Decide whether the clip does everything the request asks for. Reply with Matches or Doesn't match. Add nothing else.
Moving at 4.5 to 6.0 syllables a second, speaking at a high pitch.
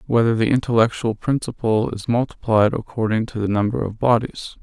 Doesn't match